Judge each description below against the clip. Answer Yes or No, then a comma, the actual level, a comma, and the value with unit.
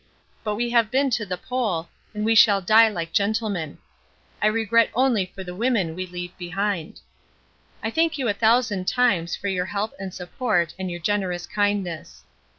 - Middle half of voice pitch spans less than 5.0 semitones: Yes, average, 4.0 semitones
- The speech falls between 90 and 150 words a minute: No, average, 175 wpm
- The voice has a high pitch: Yes, high, 205 Hz